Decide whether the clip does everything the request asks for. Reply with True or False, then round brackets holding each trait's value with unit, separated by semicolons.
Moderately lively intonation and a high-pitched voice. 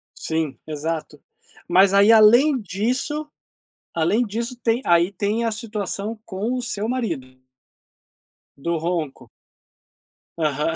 False (5.7 semitones; 200 Hz)